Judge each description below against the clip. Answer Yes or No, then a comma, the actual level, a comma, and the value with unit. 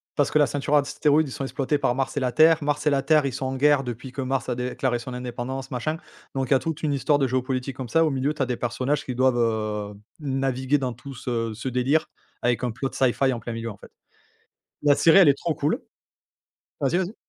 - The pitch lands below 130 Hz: No, low, 135 Hz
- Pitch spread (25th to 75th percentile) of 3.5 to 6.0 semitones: No, average, 2.7 semitones